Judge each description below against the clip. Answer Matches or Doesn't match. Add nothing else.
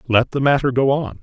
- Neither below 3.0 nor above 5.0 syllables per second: Doesn't match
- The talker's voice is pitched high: Doesn't match